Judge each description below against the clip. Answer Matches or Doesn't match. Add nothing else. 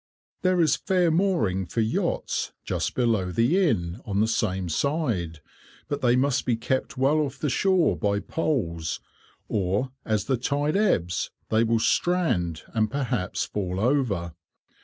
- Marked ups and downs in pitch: Matches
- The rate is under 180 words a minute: Matches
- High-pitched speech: Doesn't match